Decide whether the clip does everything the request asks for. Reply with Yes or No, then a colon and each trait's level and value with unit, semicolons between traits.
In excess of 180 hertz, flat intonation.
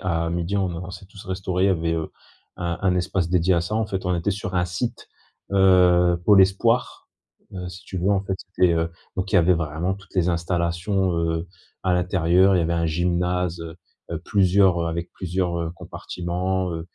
No: very low, 90 Hz; narrow, 1.8 semitones